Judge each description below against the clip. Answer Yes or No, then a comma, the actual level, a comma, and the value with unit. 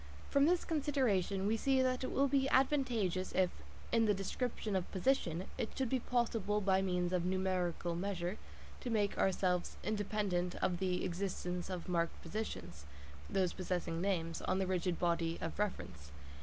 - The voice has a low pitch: No, high, 190 Hz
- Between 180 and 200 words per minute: No, average, 155 wpm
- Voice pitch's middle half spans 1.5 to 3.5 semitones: No, average, 4.0 semitones